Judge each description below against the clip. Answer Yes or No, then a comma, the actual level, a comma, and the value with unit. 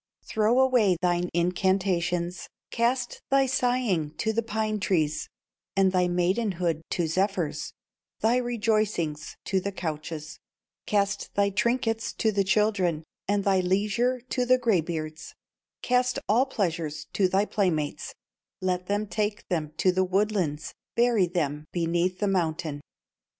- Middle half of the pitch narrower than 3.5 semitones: No, average, 4.1 semitones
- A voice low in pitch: No, high, 190 Hz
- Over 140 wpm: No, slow, 135 wpm